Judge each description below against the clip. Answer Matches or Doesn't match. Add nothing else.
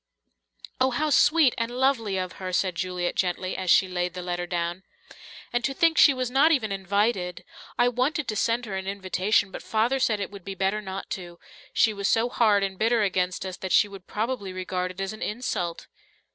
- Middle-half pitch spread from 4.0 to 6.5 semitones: Matches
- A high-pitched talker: Matches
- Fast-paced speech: Matches